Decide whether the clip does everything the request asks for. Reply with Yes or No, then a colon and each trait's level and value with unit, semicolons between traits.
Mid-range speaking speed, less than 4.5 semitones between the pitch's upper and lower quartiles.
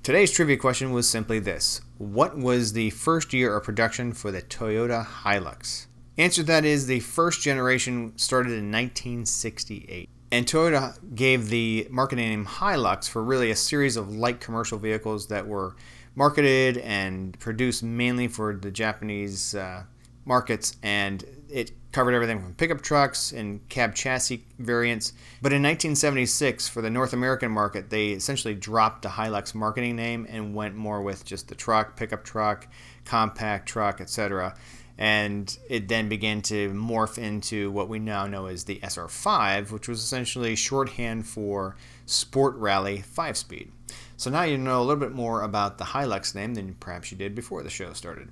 Yes: average, 165 wpm; average, 3.2 semitones